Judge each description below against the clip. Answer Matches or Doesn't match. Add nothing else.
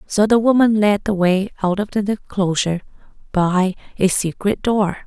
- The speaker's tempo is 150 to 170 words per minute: Matches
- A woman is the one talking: Matches